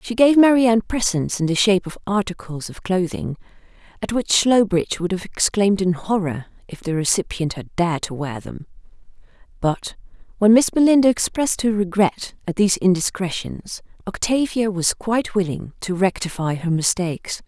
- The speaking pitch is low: No, high, 195 Hz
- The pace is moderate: Yes, average, 160 wpm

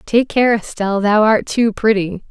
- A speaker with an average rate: Yes, average, 180 wpm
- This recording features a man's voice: No, female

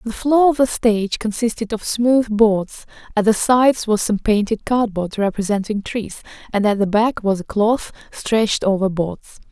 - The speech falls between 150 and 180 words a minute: Yes, average, 175 wpm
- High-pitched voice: Yes, high, 215 Hz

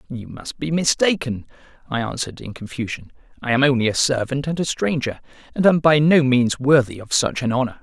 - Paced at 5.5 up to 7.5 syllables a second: Yes, 5.8 syllables/s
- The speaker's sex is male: Yes, male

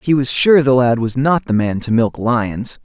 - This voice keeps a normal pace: No, fast, 255 wpm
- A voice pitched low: Yes, low, 125 Hz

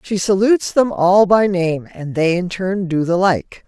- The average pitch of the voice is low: No, high, 190 Hz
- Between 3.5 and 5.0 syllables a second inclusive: Yes, 4.2 syllables/s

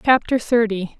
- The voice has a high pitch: Yes, high, 230 Hz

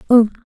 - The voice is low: No, high, 230 Hz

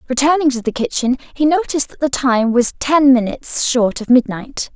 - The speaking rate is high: No, average, 190 wpm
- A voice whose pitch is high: Yes, very high, 260 Hz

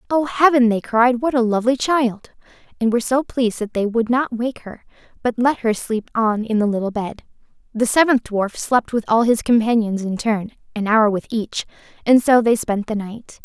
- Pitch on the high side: Yes, high, 230 Hz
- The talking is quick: Yes, fast, 210 wpm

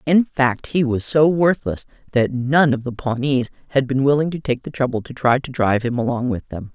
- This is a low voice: Yes, low, 130 Hz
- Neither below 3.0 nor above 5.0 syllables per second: No, 5.2 syllables/s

